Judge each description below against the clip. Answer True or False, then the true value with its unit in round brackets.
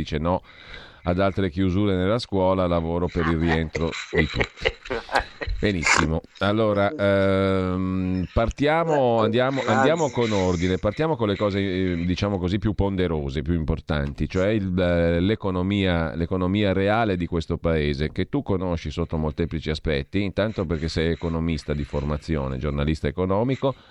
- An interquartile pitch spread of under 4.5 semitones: True (3.5 semitones)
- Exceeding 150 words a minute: False (135 wpm)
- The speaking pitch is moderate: False (90 Hz)